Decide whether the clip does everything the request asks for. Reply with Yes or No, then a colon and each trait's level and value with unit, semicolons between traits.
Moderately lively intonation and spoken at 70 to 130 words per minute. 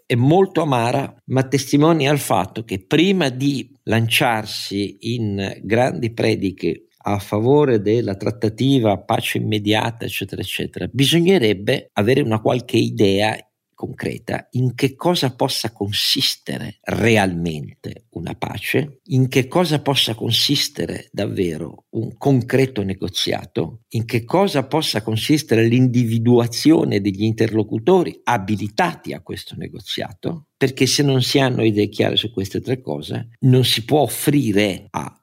Yes: average, 4.3 semitones; average, 125 wpm